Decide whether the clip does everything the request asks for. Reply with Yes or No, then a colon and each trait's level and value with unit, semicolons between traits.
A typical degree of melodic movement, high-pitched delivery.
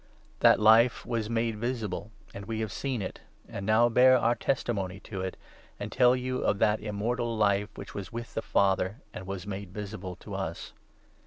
No: average, 3.0 semitones; low, 110 Hz